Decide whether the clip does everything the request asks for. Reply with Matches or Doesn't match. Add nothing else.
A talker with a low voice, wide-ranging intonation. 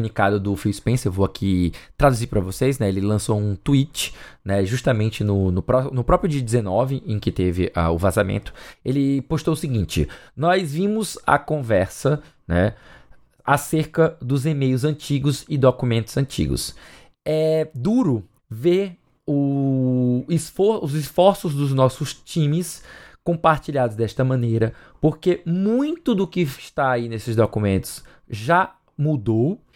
Matches